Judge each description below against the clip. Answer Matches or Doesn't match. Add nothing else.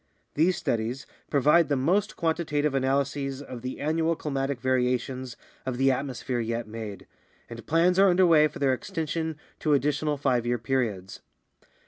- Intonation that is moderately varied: Matches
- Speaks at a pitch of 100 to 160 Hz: Matches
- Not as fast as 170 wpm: Matches